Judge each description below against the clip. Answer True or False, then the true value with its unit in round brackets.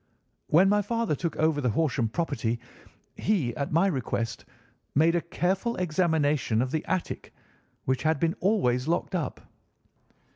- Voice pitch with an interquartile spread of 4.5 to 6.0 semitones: True (5.5 semitones)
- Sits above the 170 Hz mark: False (160 Hz)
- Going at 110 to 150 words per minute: True (145 wpm)